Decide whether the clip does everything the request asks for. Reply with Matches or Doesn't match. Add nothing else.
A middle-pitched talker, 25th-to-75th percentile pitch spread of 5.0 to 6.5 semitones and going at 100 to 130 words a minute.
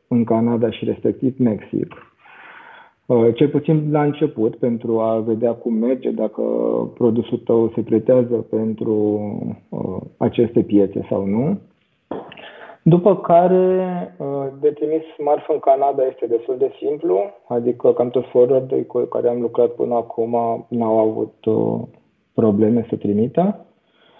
Doesn't match